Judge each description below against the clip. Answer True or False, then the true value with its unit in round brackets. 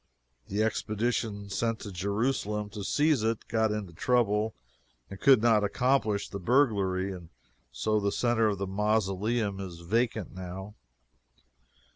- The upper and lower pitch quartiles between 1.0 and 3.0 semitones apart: True (2.7 semitones)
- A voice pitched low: True (105 Hz)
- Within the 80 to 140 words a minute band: True (135 wpm)